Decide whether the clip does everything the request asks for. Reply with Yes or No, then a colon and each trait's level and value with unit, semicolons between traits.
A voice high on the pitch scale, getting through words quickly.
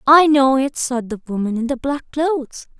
Yes: very high, 270 Hz; fast, 215 wpm